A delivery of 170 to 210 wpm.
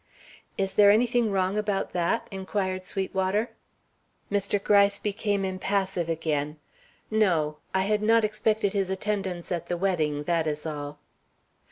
No: slow, 135 wpm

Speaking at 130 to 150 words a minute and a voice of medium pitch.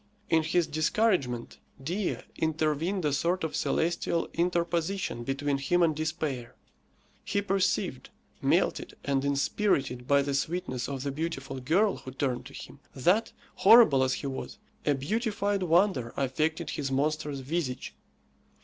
Yes: slow, 135 wpm; medium, 155 Hz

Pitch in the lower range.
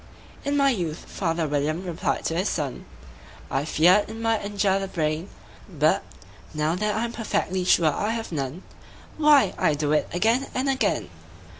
No: medium, 185 Hz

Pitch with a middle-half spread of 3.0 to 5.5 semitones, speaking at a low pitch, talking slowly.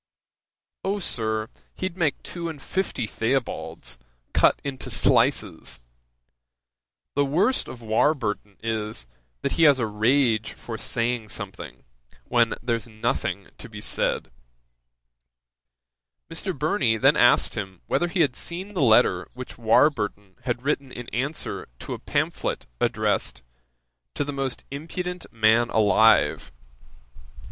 Yes: average, 5.2 semitones; low, 125 Hz; slow, 125 wpm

